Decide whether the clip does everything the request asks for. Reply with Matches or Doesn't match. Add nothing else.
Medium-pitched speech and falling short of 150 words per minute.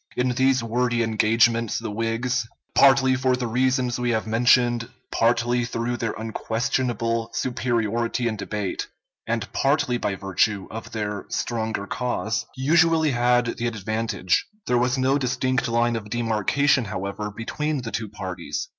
Doesn't match